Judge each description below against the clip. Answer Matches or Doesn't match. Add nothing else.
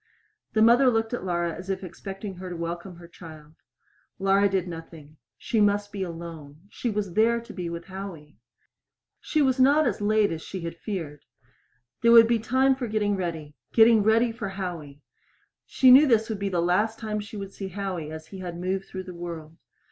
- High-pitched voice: Matches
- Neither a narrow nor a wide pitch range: Matches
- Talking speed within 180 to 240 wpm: Matches